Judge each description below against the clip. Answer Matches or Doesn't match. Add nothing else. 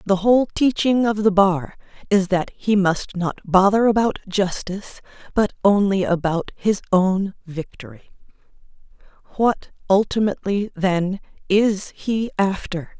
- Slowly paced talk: Matches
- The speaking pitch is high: Matches